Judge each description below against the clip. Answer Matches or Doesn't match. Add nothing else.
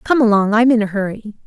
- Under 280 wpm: Doesn't match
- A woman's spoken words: Matches